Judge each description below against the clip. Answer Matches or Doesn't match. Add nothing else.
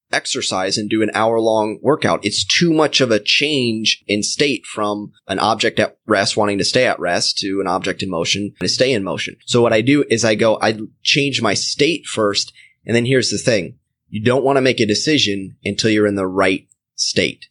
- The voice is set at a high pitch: Doesn't match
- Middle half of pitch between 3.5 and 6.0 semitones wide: Doesn't match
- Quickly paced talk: Matches